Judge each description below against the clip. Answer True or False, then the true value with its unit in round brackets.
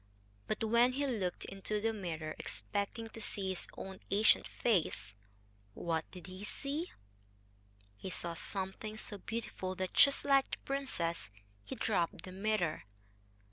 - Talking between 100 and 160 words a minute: True (140 wpm)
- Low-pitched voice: False (195 Hz)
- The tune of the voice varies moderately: True (4.3 semitones)